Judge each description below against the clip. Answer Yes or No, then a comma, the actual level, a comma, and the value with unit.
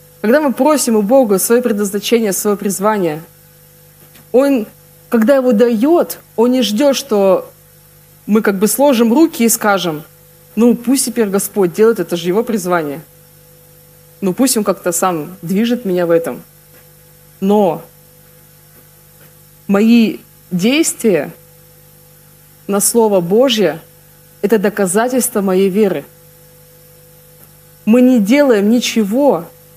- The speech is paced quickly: No, average, 115 wpm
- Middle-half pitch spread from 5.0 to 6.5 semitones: Yes, wide, 5.6 semitones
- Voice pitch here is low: No, high, 190 Hz